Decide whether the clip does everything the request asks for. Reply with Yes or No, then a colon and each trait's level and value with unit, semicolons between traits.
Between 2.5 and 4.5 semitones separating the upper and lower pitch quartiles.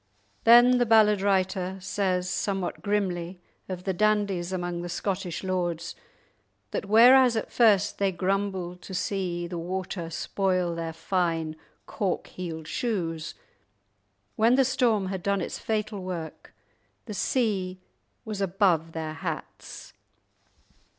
Yes: average, 2.9 semitones